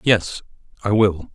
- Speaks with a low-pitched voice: Yes, low, 100 Hz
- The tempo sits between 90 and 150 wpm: Yes, slow, 135 wpm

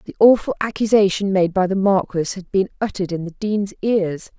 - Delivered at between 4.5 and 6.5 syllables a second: Yes, 5.5 syllables/s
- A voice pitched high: Yes, high, 195 Hz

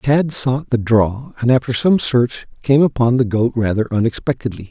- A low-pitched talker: Yes, low, 120 Hz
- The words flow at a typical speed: Yes, average, 180 wpm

